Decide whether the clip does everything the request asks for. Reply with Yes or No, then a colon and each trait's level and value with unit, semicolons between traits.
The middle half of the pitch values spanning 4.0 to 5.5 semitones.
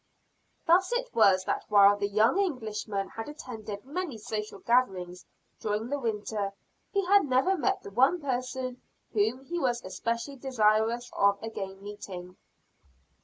Yes: average, 4.7 semitones